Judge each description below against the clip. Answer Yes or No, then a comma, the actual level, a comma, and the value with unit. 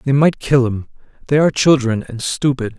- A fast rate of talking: No, average, 195 wpm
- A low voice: Yes, low, 130 Hz